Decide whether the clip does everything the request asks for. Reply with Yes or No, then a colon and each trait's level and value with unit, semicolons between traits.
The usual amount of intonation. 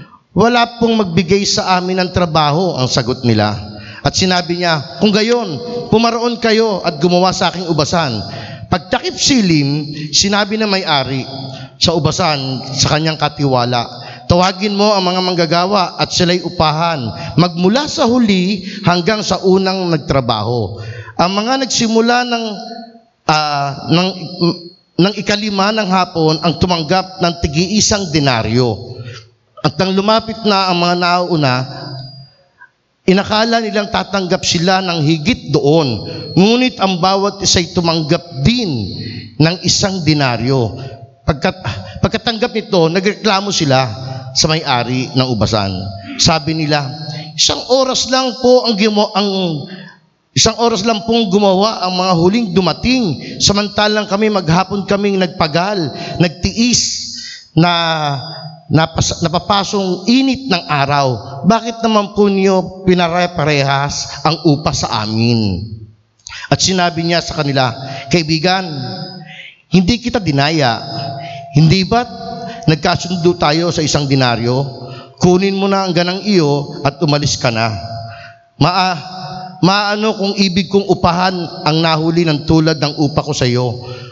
No: wide, 5.8 semitones